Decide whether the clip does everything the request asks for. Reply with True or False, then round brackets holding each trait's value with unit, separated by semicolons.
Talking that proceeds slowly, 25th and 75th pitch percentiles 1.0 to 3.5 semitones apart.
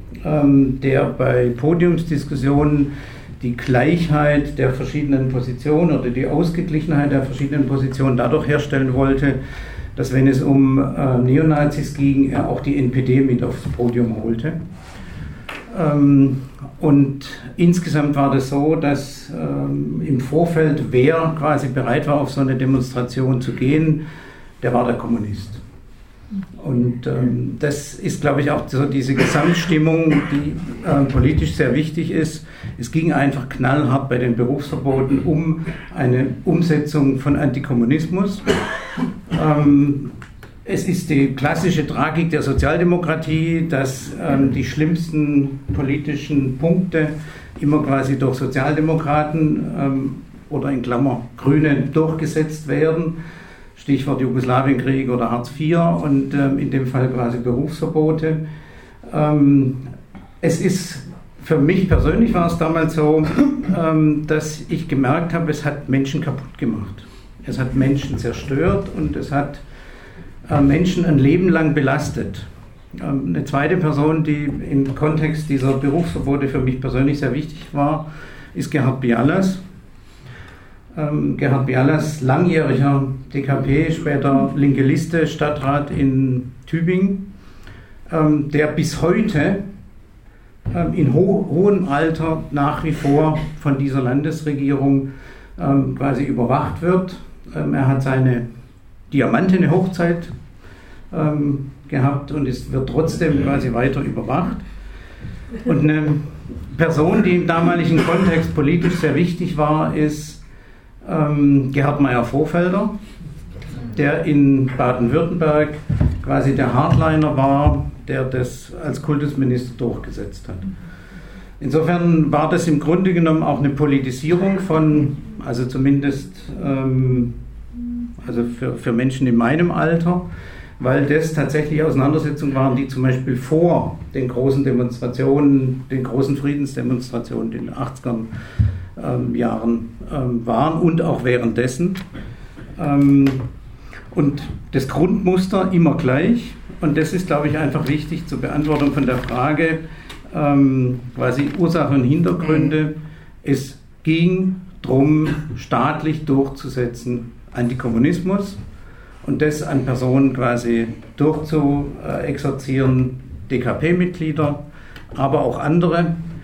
True (115 wpm; 3.1 semitones)